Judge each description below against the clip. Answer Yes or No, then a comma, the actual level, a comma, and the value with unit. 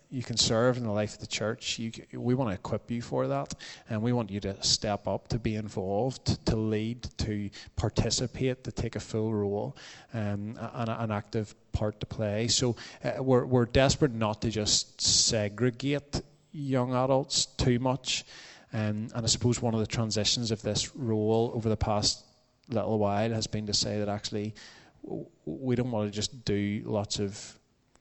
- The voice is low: Yes, low, 115 Hz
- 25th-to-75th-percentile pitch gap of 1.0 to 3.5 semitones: Yes, average, 2.8 semitones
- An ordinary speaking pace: Yes, average, 185 wpm